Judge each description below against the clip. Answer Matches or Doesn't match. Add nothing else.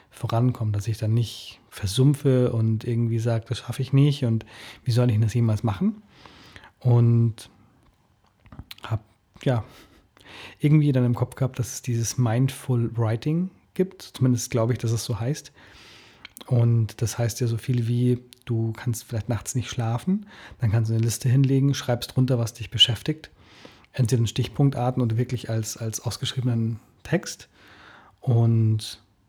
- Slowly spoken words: Doesn't match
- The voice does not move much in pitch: Matches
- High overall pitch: Doesn't match